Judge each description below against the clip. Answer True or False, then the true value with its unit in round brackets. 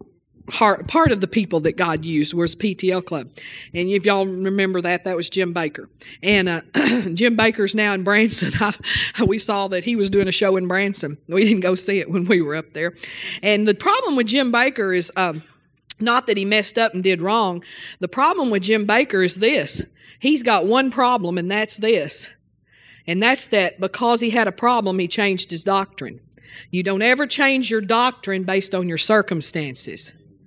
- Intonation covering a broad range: False (3.8 semitones)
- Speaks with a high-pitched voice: True (195 Hz)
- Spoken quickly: False (195 wpm)